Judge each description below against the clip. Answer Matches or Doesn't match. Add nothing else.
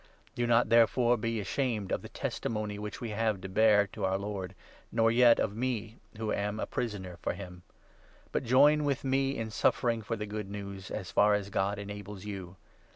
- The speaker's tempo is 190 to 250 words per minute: Matches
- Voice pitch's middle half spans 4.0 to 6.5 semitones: Doesn't match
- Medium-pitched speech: Doesn't match